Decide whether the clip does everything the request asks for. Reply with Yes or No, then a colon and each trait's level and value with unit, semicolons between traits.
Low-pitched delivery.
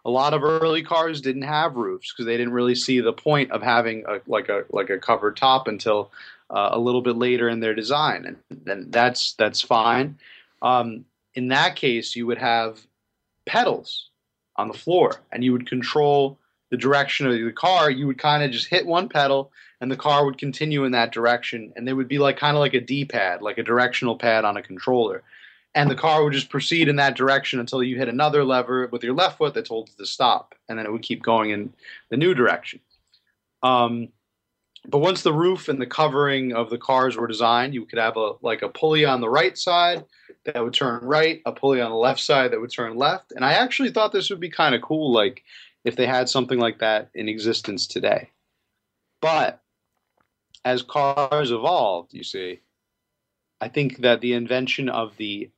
Yes: low, 130 Hz